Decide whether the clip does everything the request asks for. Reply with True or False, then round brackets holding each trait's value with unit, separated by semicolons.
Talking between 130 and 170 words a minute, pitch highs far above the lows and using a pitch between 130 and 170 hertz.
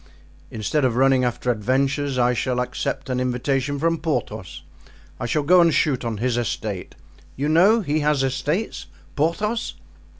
False (145 wpm; 3.6 semitones; 135 Hz)